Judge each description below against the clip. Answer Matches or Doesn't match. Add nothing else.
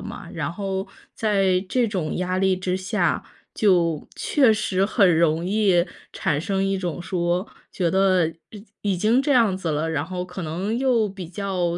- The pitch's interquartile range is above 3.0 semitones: Doesn't match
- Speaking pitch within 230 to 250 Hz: Doesn't match